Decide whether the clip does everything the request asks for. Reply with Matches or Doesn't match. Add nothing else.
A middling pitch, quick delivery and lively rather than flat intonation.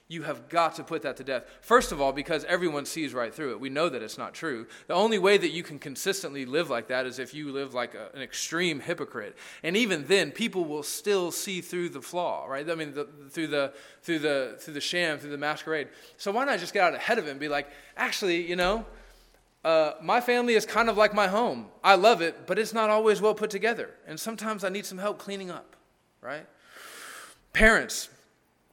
Matches